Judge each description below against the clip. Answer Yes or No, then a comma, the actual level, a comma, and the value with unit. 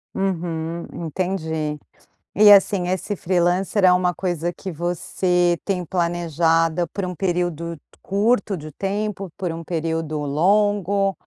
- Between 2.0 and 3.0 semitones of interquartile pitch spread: Yes, average, 2.7 semitones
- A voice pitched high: No, medium, 175 Hz